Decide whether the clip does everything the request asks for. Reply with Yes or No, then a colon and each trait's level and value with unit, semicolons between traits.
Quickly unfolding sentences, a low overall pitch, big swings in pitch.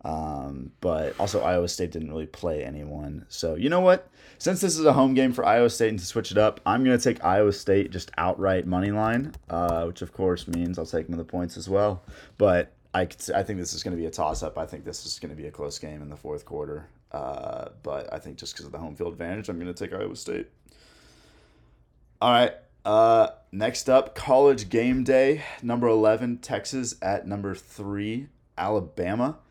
Yes: fast, 220 wpm; low, 100 Hz; wide, 6.0 semitones